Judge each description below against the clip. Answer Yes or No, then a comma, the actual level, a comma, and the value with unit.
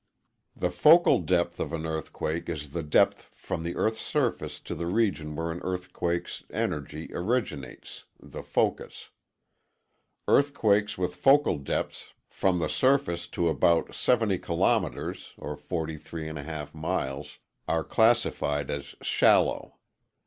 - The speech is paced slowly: Yes, slow, 120 wpm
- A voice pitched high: No, very low, 85 Hz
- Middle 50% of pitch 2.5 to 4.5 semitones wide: Yes, average, 3.7 semitones